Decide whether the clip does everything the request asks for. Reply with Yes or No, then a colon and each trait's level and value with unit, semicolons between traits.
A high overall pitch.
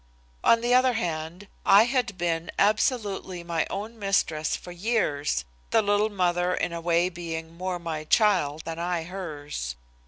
No: medium, 175 Hz